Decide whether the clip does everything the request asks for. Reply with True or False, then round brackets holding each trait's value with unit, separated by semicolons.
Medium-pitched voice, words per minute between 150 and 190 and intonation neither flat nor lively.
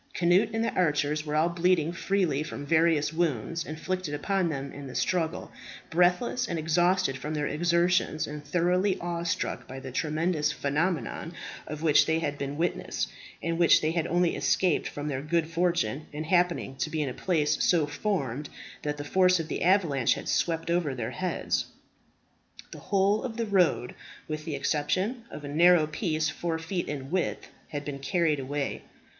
True (160 Hz; 180 wpm; 3.2 semitones)